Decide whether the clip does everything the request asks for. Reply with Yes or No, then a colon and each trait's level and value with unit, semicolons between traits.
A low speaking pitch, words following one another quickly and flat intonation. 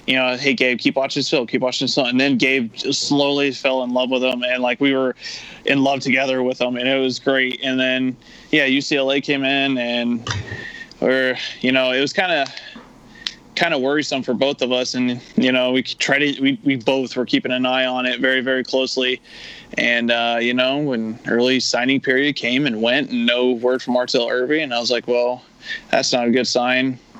Yes: low, 130 Hz; fast, 220 wpm; narrow, 1.3 semitones